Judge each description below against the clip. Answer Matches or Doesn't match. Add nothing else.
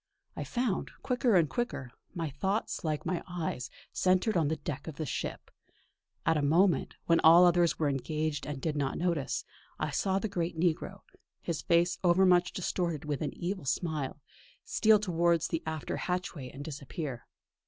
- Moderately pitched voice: Matches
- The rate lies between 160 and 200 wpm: Matches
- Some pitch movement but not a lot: Matches